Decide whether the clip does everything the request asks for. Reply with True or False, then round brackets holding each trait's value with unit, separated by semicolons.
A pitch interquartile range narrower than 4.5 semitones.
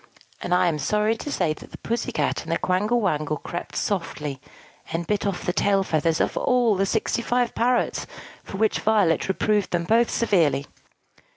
False (5.0 semitones)